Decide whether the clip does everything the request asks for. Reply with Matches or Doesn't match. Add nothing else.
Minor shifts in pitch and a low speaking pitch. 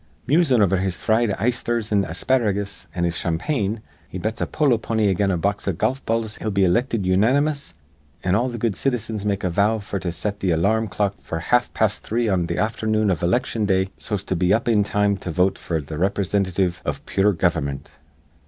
Doesn't match